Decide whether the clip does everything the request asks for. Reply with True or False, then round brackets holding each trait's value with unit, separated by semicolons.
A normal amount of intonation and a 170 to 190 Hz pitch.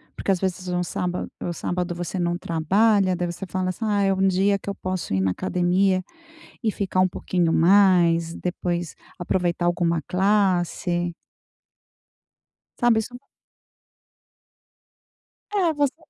False (2.1 semitones; 185 Hz)